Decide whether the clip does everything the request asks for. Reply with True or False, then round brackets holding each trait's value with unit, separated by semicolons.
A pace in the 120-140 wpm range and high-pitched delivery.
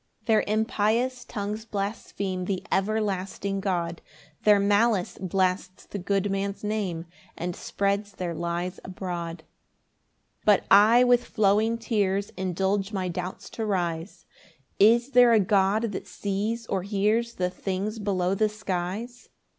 True (135 wpm; 200 Hz)